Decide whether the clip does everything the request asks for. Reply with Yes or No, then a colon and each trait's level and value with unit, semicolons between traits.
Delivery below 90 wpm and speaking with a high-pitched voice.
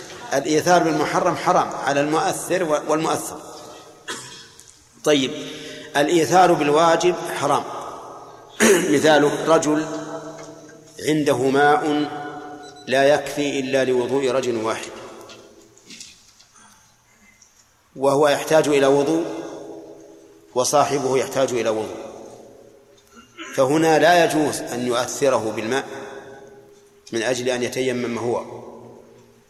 No: average, 80 wpm; medium, 145 Hz